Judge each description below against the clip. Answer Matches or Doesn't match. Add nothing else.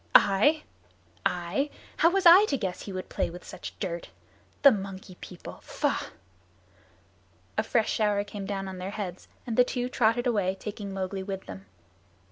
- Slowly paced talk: Doesn't match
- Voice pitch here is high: Matches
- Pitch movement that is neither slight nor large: Matches